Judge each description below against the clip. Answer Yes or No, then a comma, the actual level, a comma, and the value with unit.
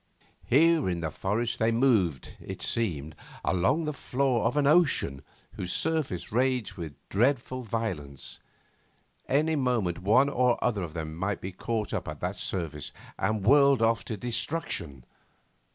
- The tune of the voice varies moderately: No, wide, 6.8 semitones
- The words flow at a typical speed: Yes, average, 150 wpm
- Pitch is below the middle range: Yes, low, 115 Hz